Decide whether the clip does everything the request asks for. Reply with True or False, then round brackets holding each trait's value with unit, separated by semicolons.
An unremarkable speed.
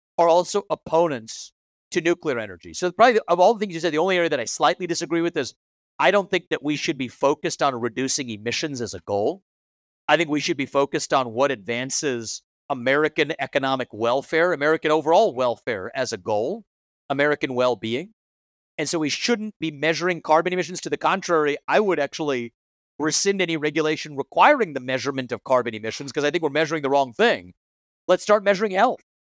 True (190 wpm)